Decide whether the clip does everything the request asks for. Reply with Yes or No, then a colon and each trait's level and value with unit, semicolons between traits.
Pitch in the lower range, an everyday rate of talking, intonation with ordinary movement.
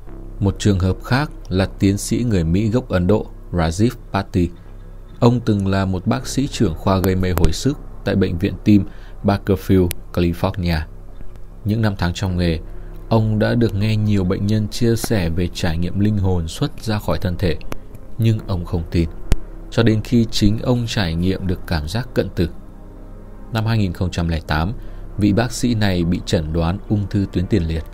Yes: low, 100 Hz; average, 185 wpm; average, 3.4 semitones